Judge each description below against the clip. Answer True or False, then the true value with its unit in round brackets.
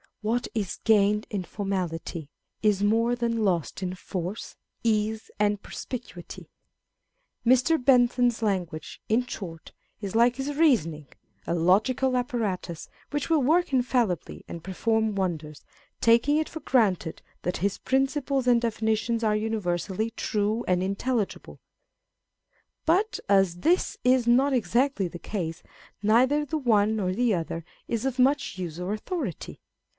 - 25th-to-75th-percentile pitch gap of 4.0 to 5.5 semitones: True (5.0 semitones)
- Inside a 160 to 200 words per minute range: False (135 wpm)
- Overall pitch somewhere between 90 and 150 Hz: False (220 Hz)